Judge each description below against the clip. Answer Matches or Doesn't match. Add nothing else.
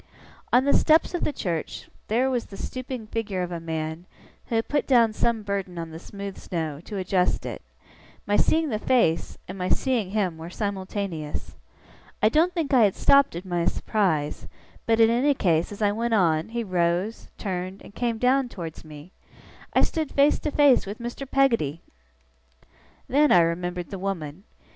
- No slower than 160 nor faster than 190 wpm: Matches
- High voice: Matches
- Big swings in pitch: Matches